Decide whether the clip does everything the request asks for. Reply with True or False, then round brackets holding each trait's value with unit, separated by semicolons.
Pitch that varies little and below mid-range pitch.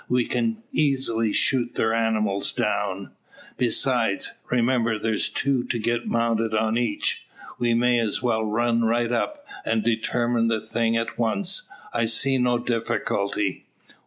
True (1.6 semitones; 115 Hz)